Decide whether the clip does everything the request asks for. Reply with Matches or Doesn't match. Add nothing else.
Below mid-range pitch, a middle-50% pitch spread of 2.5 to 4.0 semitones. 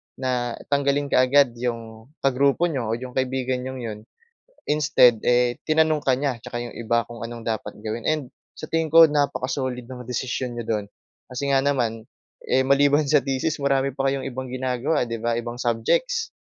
Matches